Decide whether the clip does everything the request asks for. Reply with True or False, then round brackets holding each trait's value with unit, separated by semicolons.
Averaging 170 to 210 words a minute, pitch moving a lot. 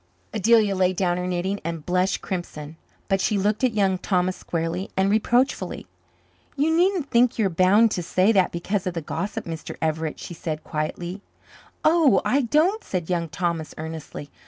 False (175 wpm; 4.2 semitones)